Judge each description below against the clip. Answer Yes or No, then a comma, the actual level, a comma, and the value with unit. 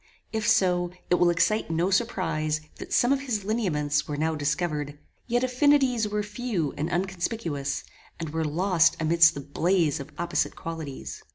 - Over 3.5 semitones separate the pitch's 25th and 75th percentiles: Yes, wide, 5.5 semitones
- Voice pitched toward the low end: No, medium, 175 Hz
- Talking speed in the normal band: Yes, average, 160 wpm